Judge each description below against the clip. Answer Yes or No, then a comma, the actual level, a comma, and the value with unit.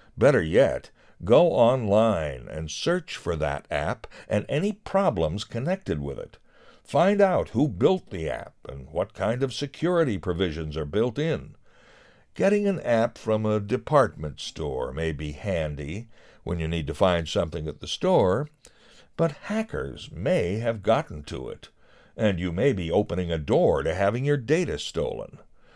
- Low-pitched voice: Yes, low, 110 Hz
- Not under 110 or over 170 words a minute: Yes, average, 160 wpm